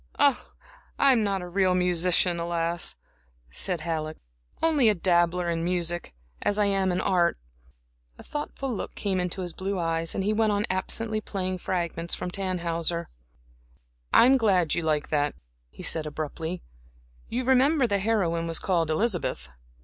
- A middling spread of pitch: Yes, average, 3.5 semitones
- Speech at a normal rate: Yes, average, 155 wpm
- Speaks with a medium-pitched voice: Yes, medium, 180 Hz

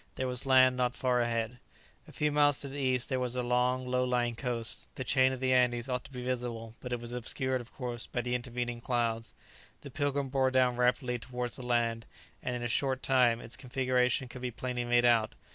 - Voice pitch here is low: Yes, low, 125 Hz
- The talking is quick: Yes, fast, 225 wpm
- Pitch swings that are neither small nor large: No, narrow, 1.2 semitones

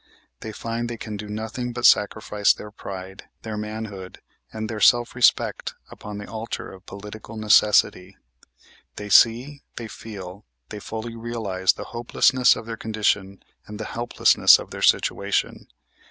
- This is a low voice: Yes, low, 110 Hz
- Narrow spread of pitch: Yes, narrow, 2.0 semitones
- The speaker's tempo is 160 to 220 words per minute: No, average, 150 wpm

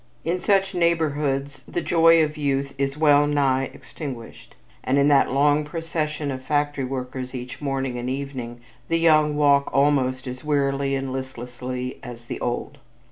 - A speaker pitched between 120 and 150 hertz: Yes, medium, 140 Hz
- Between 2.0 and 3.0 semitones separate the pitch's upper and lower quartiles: Yes, narrow, 2.5 semitones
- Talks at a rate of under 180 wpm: Yes, average, 155 wpm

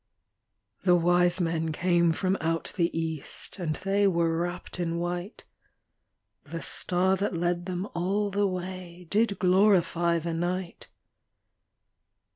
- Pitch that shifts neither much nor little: No, narrow, 1.8 semitones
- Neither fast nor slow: No, slow, 125 wpm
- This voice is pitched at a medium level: Yes, medium, 175 Hz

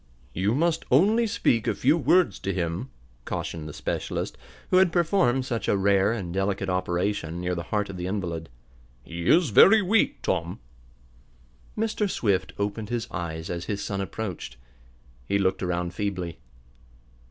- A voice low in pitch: Yes, low, 100 Hz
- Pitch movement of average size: No, wide, 6.5 semitones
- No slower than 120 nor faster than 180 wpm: Yes, average, 155 wpm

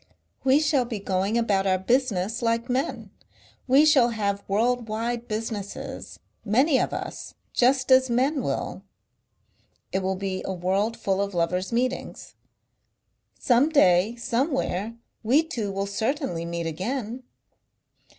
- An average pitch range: Yes, average, 4.8 semitones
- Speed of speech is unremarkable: No, slow, 130 wpm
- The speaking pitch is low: No, high, 230 Hz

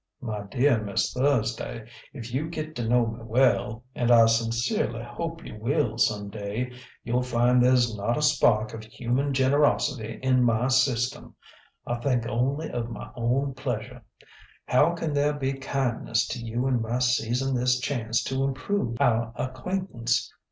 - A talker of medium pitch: No, low, 125 Hz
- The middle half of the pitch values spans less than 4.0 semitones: Yes, average, 2.8 semitones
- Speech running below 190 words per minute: Yes, average, 160 wpm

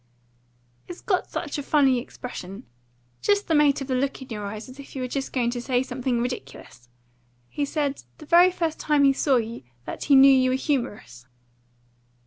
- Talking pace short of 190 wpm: No, average, 195 wpm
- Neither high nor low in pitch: No, very high, 265 Hz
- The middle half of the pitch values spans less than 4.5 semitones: Yes, average, 3.1 semitones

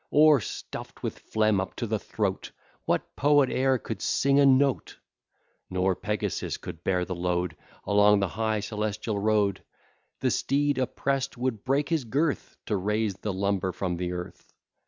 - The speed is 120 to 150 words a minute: No, average, 160 wpm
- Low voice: Yes, low, 105 Hz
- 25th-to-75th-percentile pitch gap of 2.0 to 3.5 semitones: No, wide, 5.6 semitones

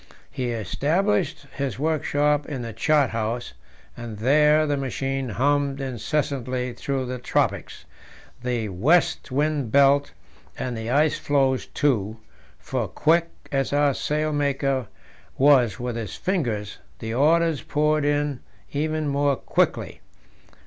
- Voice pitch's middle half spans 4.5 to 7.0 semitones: No, average, 3.2 semitones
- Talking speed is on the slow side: Yes, slow, 120 wpm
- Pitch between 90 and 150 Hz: Yes, medium, 140 Hz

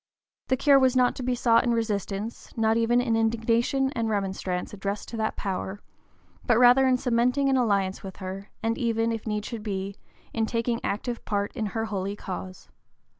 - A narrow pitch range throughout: No, average, 3.1 semitones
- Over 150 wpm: Yes, average, 185 wpm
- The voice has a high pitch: Yes, high, 225 Hz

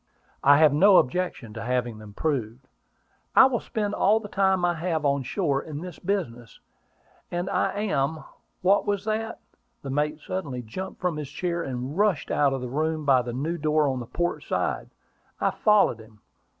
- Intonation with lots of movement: Yes, wide, 6.1 semitones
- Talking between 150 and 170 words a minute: No, average, 185 wpm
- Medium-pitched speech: Yes, medium, 155 Hz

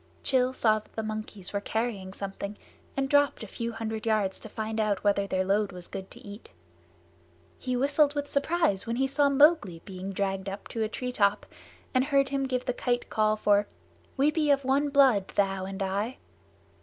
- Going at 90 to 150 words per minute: No, average, 195 wpm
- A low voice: No, high, 220 Hz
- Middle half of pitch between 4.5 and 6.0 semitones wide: Yes, average, 5.1 semitones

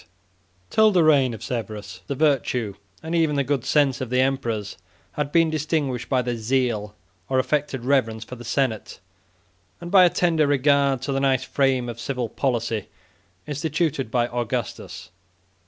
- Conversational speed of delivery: Yes, average, 165 wpm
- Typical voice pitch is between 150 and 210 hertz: No, low, 130 Hz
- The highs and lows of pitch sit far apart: No, average, 3.6 semitones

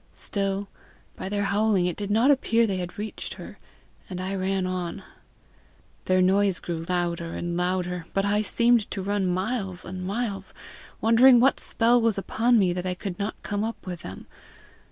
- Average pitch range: Yes, average, 3.1 semitones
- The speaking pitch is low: No, high, 195 Hz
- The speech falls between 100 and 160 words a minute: No, average, 175 wpm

